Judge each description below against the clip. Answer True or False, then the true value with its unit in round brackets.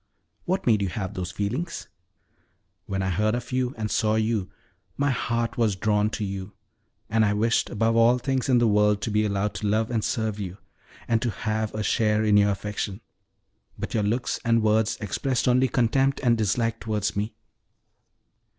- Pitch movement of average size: False (2.1 semitones)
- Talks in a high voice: False (110 Hz)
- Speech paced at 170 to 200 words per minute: True (185 wpm)